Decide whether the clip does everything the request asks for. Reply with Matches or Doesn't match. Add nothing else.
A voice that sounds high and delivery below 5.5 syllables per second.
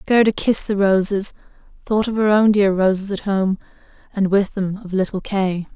Matches